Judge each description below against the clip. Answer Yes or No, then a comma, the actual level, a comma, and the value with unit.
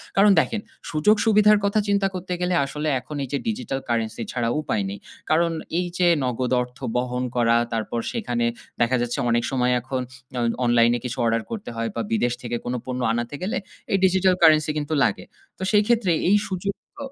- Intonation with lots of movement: Yes, wide, 8.3 semitones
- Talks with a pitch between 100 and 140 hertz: Yes, low, 135 Hz